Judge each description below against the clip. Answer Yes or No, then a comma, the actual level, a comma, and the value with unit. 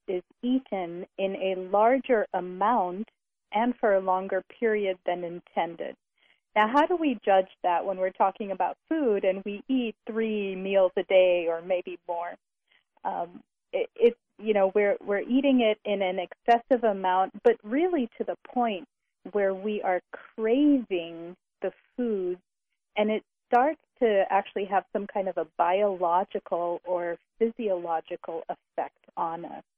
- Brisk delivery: No, average, 150 wpm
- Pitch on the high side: Yes, high, 200 Hz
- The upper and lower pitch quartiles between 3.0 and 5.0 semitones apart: Yes, average, 3.8 semitones